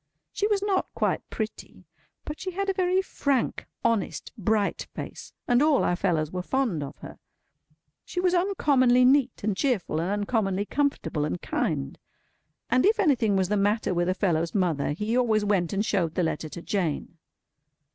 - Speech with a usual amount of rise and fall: No, wide, 7.6 semitones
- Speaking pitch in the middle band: No, high, 210 Hz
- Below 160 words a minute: No, average, 175 wpm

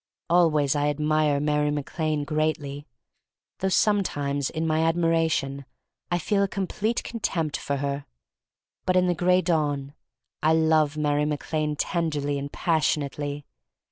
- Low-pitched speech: No, medium, 155 Hz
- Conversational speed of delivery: Yes, average, 145 wpm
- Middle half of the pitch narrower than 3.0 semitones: Yes, narrow, 2.4 semitones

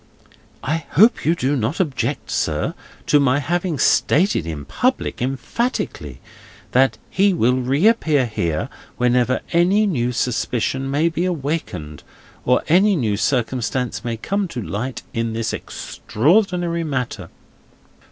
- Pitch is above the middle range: No, low, 135 Hz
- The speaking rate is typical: No, slow, 125 wpm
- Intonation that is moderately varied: No, wide, 6.2 semitones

